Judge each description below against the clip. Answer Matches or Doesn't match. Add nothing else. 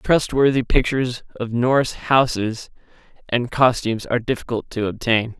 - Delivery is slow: Matches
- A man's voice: Matches